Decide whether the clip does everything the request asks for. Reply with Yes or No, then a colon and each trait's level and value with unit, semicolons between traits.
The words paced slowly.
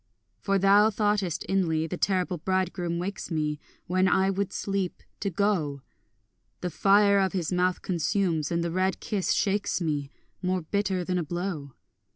No: average, 160 wpm